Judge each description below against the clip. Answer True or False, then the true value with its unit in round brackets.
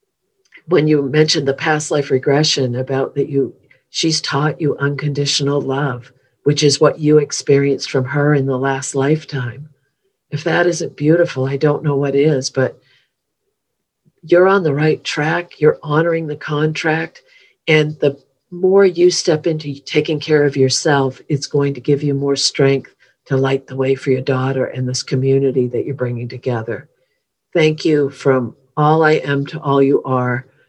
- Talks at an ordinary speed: True (170 wpm)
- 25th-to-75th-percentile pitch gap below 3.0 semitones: True (2.4 semitones)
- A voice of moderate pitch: True (145 Hz)